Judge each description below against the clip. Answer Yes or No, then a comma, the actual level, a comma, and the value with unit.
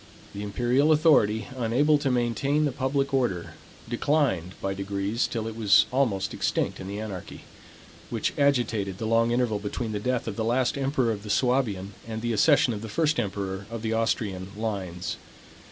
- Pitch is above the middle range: No, low, 115 Hz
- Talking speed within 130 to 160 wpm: No, average, 175 wpm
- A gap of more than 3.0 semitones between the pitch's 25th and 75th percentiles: Yes, average, 4.3 semitones